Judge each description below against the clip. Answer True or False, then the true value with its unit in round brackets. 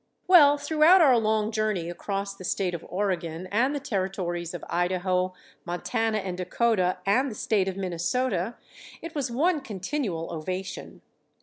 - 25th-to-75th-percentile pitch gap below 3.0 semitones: False (5.4 semitones)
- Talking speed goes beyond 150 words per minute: False (145 wpm)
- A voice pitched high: True (195 Hz)